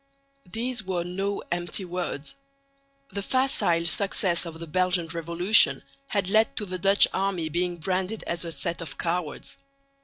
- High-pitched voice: No, medium, 180 Hz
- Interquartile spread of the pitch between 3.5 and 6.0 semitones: No, average, 2.7 semitones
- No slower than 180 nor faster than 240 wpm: No, average, 150 wpm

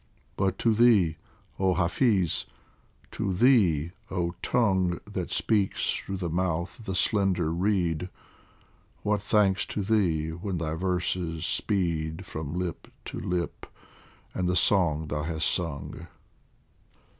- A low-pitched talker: Yes, very low, 90 Hz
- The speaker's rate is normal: No, slow, 125 wpm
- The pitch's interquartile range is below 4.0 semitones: Yes, average, 3.0 semitones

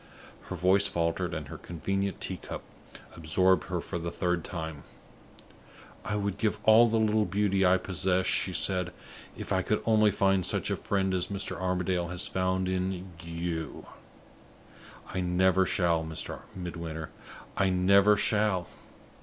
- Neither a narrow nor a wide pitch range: No, narrow, 2.1 semitones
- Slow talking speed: No, average, 150 wpm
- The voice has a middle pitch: No, very low, 95 Hz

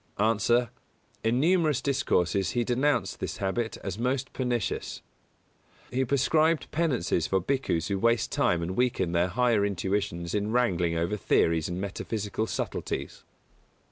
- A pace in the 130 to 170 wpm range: Yes, average, 140 wpm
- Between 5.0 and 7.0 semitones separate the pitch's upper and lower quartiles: Yes, average, 5.3 semitones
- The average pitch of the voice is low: Yes, low, 110 Hz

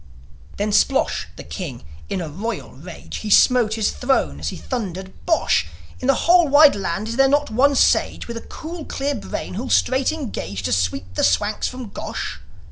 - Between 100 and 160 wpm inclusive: No, average, 190 wpm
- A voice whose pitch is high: Yes, high, 220 Hz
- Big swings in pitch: Yes, wide, 7.1 semitones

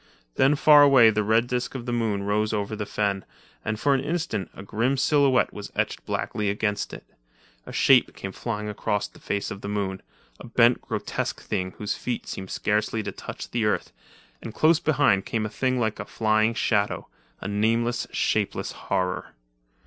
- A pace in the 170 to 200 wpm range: Yes, average, 185 wpm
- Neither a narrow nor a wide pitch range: Yes, average, 3.3 semitones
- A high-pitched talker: No, low, 110 Hz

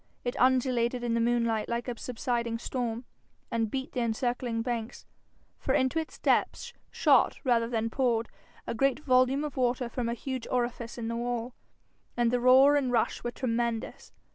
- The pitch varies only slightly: Yes, narrow, 1.6 semitones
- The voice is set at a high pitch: Yes, high, 240 Hz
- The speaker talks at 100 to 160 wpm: No, average, 175 wpm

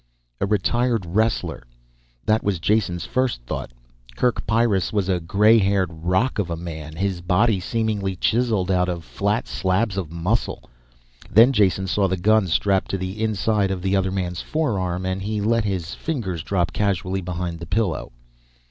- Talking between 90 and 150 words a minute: No, average, 165 wpm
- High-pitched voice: No, very low, 95 Hz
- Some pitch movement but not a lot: Yes, average, 3.3 semitones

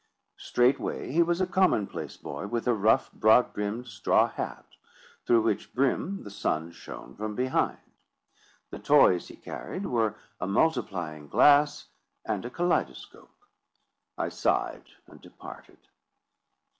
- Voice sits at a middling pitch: No, low, 120 Hz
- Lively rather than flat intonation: Yes, wide, 6.1 semitones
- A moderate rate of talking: No, slow, 130 wpm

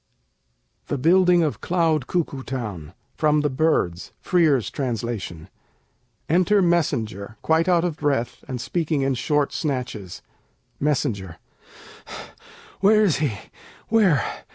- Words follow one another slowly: Yes, slow, 115 wpm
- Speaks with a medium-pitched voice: Yes, medium, 145 Hz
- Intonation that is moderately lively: No, wide, 6.1 semitones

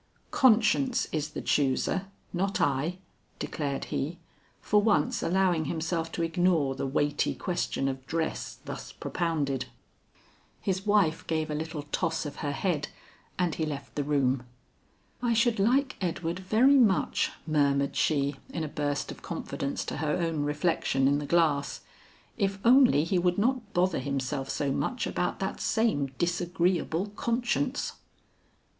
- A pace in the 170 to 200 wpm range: No, average, 145 wpm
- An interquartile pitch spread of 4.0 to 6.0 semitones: Yes, average, 4.9 semitones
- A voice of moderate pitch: Yes, medium, 165 Hz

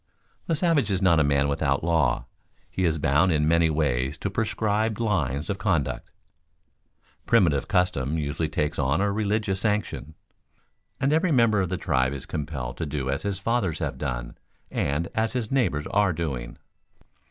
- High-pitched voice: No, very low, 85 Hz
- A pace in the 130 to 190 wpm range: Yes, average, 170 wpm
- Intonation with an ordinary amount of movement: No, wide, 6.4 semitones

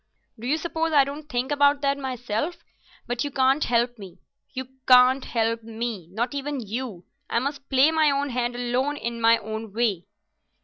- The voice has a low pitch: No, very high, 250 Hz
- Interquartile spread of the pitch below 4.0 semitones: Yes, average, 3.6 semitones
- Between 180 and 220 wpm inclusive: No, average, 170 wpm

